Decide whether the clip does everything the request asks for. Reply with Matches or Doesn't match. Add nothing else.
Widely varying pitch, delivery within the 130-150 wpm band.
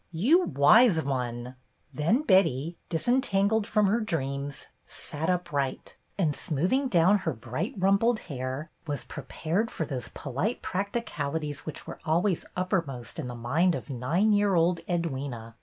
Matches